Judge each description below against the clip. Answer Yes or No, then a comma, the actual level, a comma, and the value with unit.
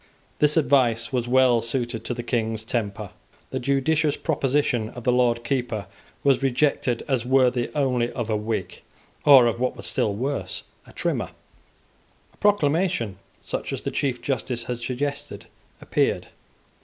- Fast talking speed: No, average, 150 wpm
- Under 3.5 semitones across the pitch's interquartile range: Yes, average, 3.0 semitones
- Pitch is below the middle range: Yes, low, 125 Hz